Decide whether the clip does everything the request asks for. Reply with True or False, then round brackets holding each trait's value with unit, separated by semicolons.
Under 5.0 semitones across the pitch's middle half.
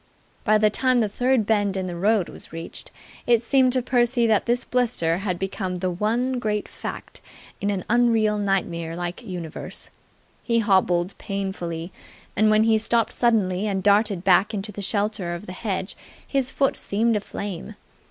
True (3.7 semitones)